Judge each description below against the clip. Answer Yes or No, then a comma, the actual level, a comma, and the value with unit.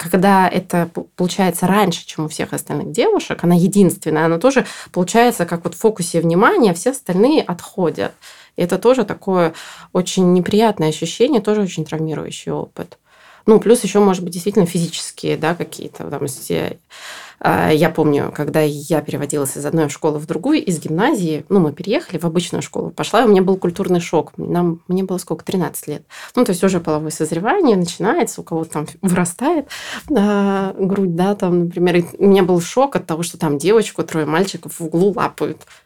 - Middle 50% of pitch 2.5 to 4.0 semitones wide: Yes, average, 3.5 semitones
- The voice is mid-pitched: Yes, medium, 180 Hz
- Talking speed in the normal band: No, fast, 175 wpm